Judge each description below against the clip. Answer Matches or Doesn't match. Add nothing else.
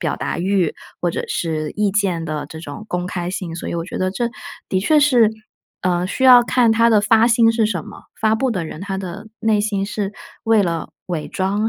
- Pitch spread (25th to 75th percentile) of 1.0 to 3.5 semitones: Doesn't match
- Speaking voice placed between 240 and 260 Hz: Doesn't match